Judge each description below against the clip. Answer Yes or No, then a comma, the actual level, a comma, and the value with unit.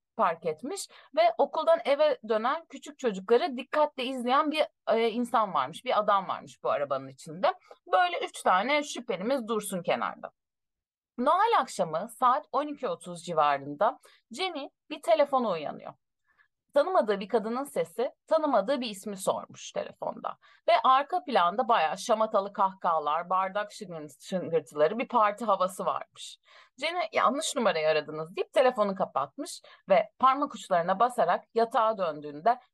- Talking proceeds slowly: No, average, 125 wpm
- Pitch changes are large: Yes, wide, 7.6 semitones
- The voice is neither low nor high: No, high, 245 Hz